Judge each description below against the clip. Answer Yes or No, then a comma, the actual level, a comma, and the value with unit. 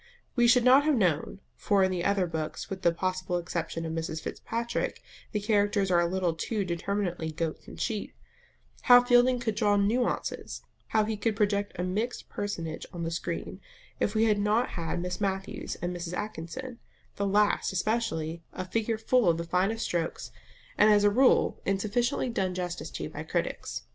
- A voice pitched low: No, high, 200 Hz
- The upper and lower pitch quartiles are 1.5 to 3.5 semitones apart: No, average, 4.1 semitones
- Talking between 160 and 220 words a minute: Yes, average, 180 wpm